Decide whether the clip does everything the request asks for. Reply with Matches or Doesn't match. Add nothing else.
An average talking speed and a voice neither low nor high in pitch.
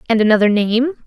Doesn't match